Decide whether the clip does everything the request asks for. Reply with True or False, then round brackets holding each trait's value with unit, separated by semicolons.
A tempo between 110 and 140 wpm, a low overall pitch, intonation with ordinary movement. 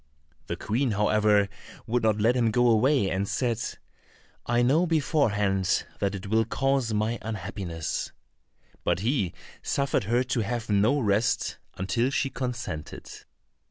True (135 wpm; 115 Hz; 3.4 semitones)